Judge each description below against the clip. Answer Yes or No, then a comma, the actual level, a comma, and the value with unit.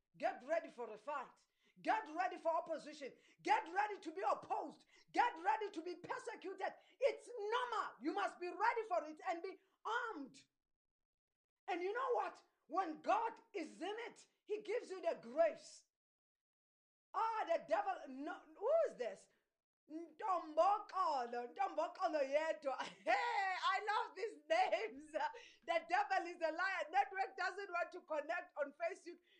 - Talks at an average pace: Yes, average, 145 wpm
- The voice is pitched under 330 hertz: No, very high, 360 Hz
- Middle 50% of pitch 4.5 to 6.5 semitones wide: No, average, 4.0 semitones